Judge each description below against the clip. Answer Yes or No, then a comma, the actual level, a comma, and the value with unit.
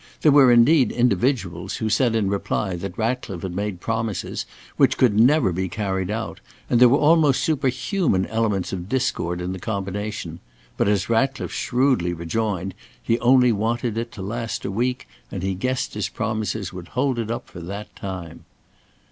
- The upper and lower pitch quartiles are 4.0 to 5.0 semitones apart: Yes, average, 4.6 semitones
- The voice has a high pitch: No, low, 110 Hz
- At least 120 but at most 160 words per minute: No, average, 175 wpm